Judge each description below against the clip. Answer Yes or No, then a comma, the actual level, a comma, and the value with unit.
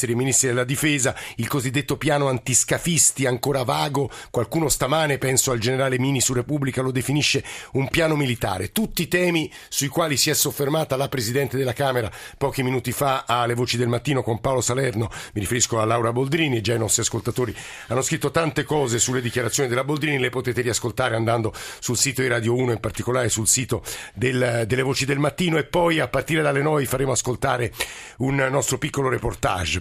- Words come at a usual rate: No, fast, 185 wpm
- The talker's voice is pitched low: Yes, low, 130 Hz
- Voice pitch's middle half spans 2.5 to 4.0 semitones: Yes, average, 2.8 semitones